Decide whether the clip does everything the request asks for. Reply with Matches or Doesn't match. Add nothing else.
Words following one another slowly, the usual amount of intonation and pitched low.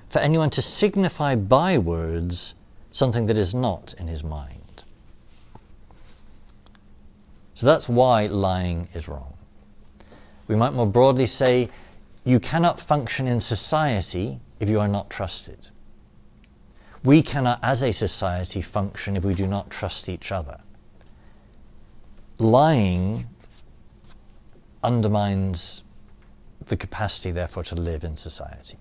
Doesn't match